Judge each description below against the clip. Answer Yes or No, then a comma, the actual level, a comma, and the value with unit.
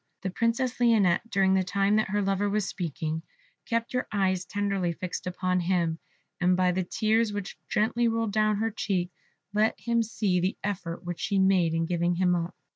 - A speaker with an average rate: Yes, average, 190 wpm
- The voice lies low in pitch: No, high, 195 Hz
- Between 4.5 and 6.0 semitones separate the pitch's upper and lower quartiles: No, average, 3.1 semitones